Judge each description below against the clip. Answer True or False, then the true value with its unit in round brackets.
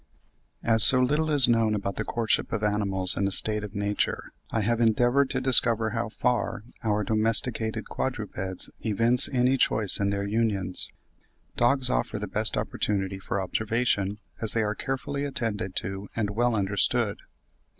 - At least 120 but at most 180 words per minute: True (160 wpm)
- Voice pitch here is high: False (110 Hz)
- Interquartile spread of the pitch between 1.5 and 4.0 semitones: True (3.0 semitones)